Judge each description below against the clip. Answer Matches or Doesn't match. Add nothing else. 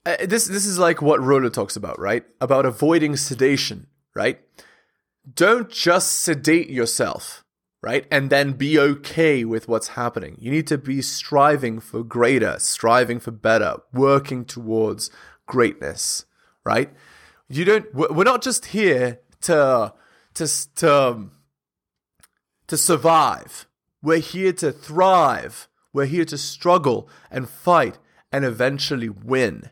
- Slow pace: Matches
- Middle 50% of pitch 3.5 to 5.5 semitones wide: Matches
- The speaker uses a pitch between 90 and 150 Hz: Matches